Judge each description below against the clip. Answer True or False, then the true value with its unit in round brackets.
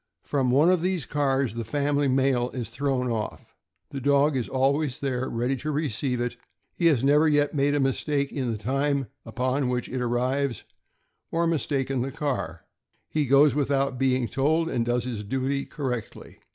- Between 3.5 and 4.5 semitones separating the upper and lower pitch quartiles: False (2.6 semitones)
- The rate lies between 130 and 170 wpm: False (180 wpm)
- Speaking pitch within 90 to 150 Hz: True (135 Hz)